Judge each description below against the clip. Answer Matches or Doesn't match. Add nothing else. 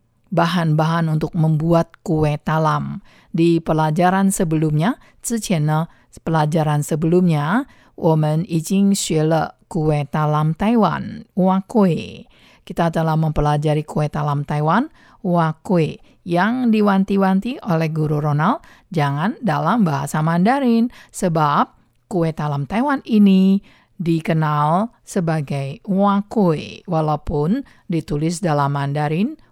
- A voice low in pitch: Doesn't match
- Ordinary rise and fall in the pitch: Matches